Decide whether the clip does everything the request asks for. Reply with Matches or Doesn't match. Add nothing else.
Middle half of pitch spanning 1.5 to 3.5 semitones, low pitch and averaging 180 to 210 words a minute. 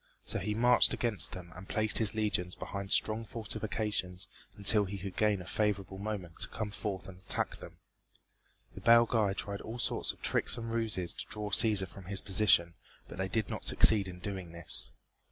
Matches